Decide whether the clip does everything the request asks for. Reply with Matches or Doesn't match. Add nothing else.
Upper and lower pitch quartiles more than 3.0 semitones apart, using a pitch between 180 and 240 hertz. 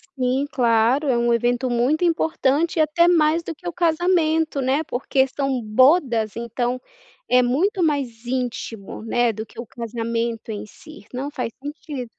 Doesn't match